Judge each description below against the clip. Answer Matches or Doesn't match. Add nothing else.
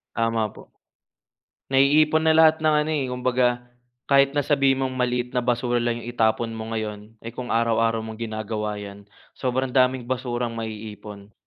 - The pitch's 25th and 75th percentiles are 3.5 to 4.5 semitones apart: Doesn't match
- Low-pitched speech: Matches